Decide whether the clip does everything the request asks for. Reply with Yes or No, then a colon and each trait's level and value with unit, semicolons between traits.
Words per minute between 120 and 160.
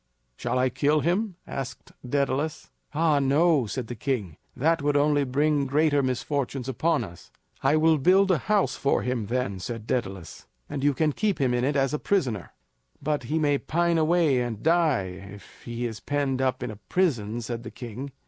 No: average, 185 wpm